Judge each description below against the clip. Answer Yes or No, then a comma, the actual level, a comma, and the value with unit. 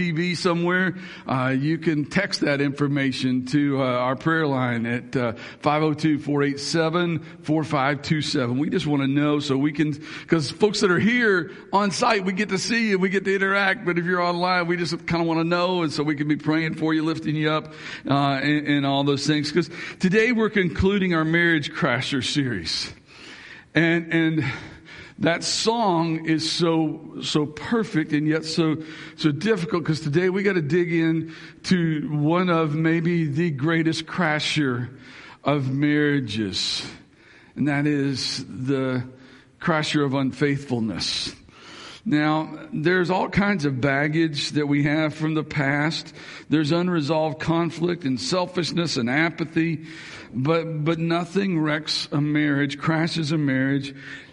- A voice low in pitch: No, medium, 155 Hz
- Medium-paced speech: Yes, average, 155 wpm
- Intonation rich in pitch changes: No, average, 2.9 semitones